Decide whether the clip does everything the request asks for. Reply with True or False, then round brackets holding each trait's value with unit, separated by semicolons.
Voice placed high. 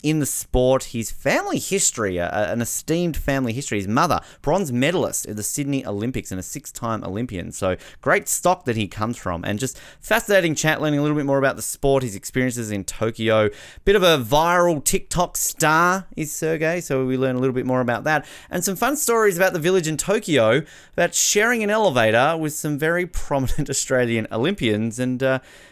False (140 Hz)